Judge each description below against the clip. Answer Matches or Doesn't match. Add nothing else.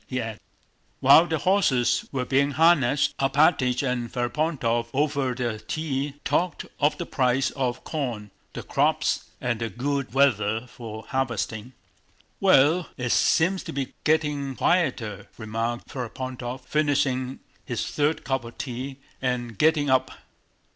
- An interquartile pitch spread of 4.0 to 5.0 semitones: Doesn't match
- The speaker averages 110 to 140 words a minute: Matches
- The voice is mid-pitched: Doesn't match